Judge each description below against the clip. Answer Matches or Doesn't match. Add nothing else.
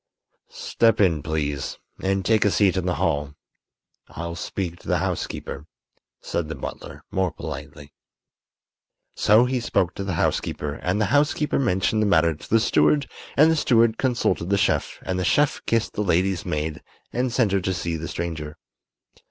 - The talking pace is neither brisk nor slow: Matches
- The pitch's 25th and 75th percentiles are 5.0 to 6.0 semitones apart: Matches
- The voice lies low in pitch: Matches